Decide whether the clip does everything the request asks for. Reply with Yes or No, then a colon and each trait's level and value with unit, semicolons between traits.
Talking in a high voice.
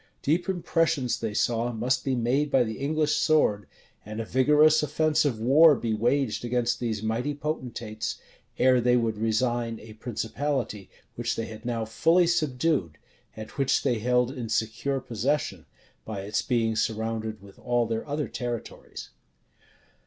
No: low, 120 Hz